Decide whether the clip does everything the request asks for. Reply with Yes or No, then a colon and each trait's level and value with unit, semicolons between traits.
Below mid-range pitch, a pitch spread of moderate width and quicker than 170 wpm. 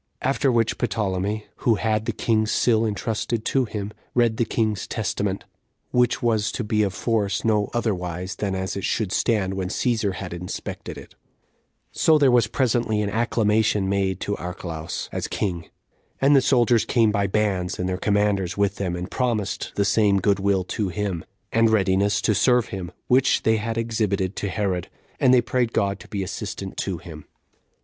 Yes: low, 105 Hz; average, 3.0 semitones; average, 180 wpm